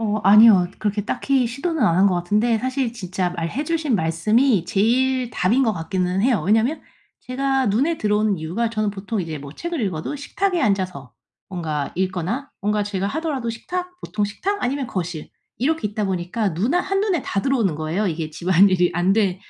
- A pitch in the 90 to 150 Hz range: No, high, 210 Hz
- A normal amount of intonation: No, wide, 6.0 semitones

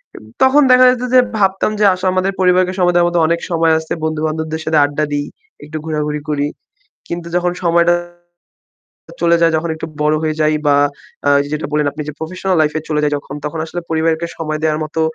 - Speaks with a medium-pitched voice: Yes, medium, 160 Hz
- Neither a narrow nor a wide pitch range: No, narrow, 2.3 semitones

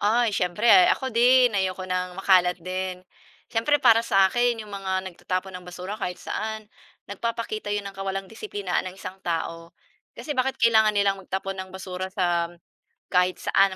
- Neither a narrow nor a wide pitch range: Yes, average, 3.1 semitones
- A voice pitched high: Yes, high, 195 Hz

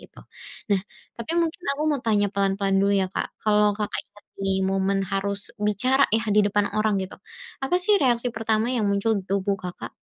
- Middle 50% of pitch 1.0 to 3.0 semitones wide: Yes, narrow, 2.4 semitones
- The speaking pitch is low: No, high, 210 Hz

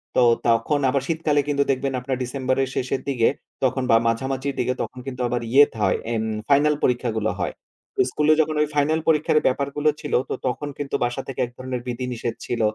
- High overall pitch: No, low, 130 Hz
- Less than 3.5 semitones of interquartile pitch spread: Yes, average, 2.7 semitones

